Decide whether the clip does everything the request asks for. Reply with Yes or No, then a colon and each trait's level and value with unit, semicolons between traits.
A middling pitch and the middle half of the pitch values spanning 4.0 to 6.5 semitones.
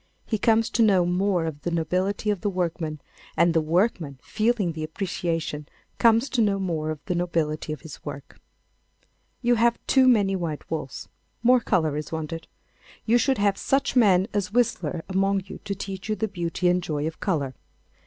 Yes: medium, 180 Hz; average, 4.7 semitones